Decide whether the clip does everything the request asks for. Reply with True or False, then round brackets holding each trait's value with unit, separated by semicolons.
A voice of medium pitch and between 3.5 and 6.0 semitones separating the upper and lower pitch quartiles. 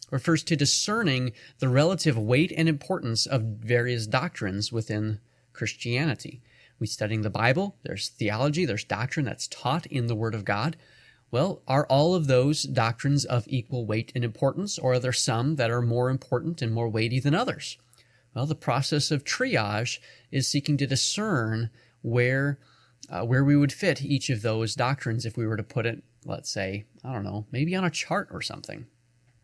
False (125 Hz; 4.1 semitones)